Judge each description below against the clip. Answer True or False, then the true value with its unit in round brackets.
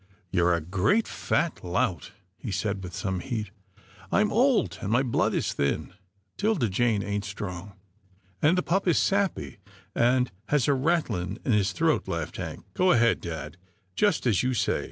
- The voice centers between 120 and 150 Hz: False (105 Hz)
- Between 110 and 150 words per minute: False (195 wpm)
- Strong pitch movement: True (6.6 semitones)